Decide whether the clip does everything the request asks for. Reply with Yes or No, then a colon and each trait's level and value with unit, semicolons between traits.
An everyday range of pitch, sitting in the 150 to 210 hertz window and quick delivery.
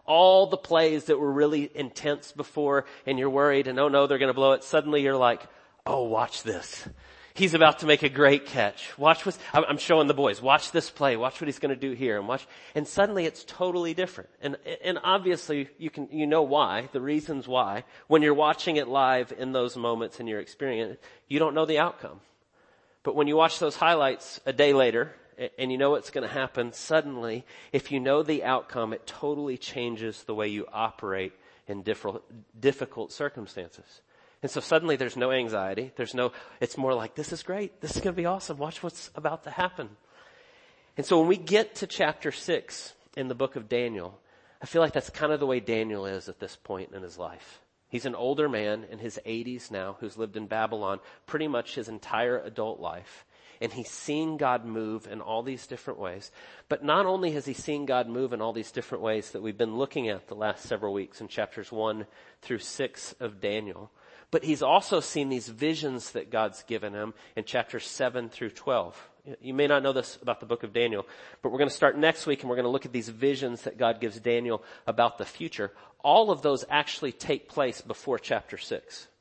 No: average, 4.4 semitones; low, 135 Hz; fast, 210 wpm